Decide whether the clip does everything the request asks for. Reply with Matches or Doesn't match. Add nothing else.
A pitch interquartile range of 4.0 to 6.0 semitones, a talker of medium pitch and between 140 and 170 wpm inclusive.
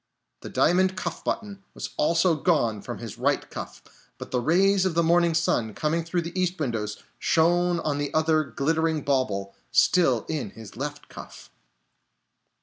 Matches